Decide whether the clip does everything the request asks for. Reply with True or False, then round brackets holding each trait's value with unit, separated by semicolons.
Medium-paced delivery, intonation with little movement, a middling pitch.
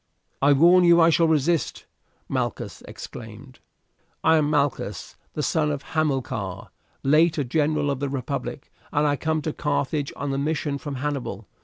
True (160 wpm; 2.3 semitones; 145 Hz)